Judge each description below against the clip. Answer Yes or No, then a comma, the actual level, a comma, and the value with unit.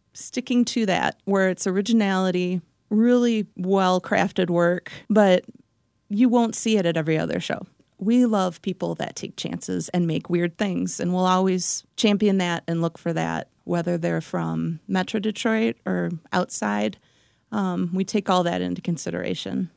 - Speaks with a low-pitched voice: No, medium, 180 Hz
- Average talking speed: Yes, average, 160 wpm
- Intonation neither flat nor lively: Yes, average, 4.6 semitones